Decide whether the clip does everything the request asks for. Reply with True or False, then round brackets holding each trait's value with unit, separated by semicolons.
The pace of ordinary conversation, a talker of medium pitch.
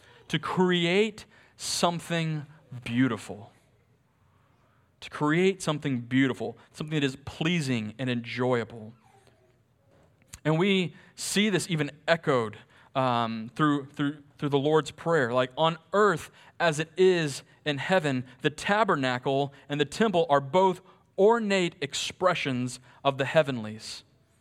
False (115 wpm; 145 Hz)